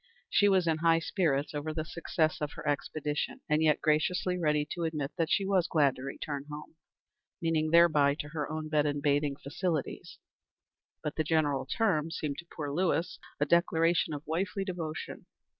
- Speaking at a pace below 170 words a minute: No, average, 175 wpm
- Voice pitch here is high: No, medium, 155 Hz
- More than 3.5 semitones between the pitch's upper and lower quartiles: No, narrow, 2.4 semitones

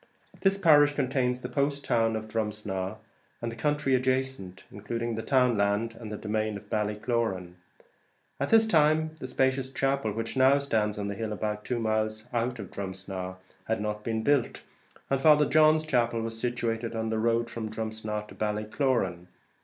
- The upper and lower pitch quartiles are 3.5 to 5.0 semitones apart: Yes, average, 3.8 semitones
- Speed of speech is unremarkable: Yes, average, 170 wpm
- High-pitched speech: No, low, 115 Hz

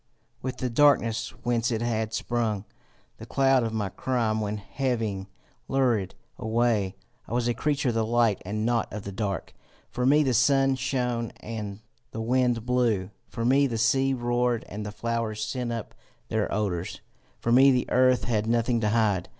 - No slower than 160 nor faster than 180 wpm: Yes, average, 175 wpm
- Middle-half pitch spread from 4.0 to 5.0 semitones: No, narrow, 2.6 semitones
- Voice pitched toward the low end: Yes, low, 115 Hz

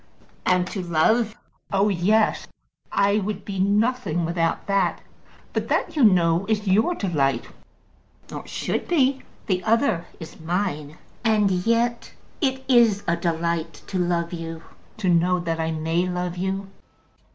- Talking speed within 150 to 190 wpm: No, average, 140 wpm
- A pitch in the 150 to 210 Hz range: Yes, medium, 185 Hz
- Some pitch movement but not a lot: Yes, average, 4.0 semitones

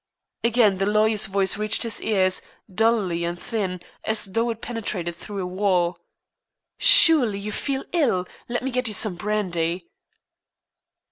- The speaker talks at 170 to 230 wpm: No, average, 145 wpm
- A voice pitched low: No, high, 210 Hz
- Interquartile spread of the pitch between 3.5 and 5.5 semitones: Yes, average, 3.8 semitones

